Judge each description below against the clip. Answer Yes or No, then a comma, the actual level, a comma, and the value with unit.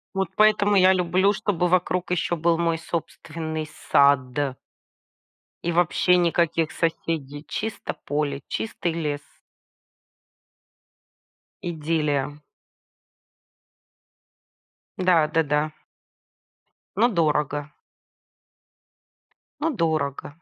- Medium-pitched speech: Yes, medium, 165 Hz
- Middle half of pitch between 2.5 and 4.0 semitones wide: Yes, average, 3.2 semitones